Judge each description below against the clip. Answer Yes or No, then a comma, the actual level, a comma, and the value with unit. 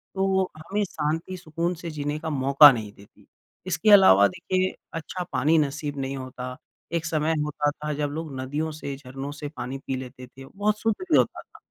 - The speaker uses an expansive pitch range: No, average, 4.0 semitones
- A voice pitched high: No, medium, 150 Hz